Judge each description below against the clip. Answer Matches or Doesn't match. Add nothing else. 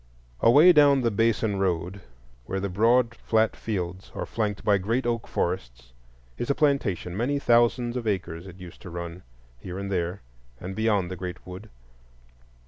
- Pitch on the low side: Matches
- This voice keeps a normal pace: Matches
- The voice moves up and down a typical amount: Matches